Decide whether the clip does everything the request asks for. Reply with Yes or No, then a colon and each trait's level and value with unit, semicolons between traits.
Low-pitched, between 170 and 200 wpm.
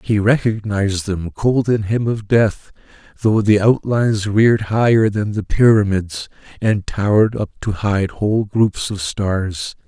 No: low, 105 Hz; average, 150 wpm